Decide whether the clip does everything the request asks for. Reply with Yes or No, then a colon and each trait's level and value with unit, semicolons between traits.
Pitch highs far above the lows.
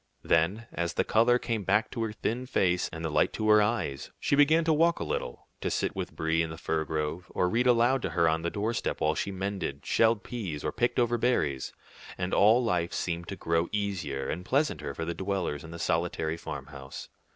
Yes: wide, 5.9 semitones